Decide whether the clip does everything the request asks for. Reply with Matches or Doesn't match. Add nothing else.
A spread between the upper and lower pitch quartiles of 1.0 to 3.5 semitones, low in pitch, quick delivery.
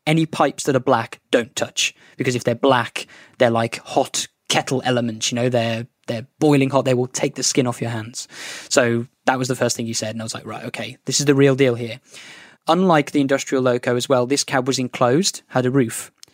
Matches